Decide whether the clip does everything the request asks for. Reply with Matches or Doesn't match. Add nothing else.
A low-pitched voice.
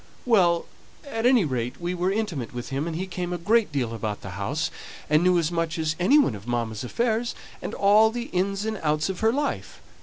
Doesn't match